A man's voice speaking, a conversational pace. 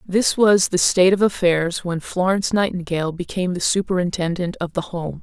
No: female; average, 170 wpm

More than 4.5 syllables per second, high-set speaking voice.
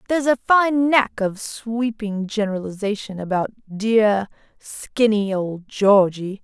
No: 4.4 syllables/s; high, 215 Hz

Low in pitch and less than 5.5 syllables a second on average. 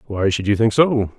Yes: low, 110 Hz; 5.0 syllables/s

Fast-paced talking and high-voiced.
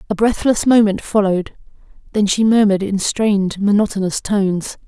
No: slow, 135 wpm; high, 205 Hz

